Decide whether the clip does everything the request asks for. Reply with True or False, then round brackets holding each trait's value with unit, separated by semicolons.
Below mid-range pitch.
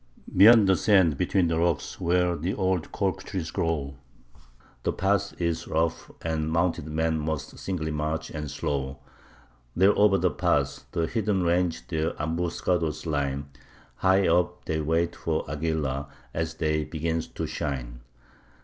True (80 Hz)